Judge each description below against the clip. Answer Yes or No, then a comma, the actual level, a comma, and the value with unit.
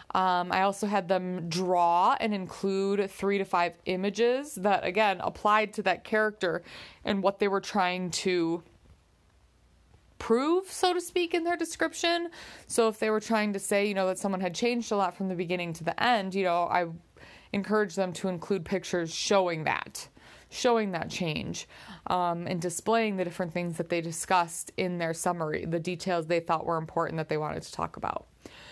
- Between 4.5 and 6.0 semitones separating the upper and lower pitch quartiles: No, average, 3.5 semitones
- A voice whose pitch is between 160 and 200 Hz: Yes, medium, 185 Hz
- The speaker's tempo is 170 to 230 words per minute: Yes, average, 190 wpm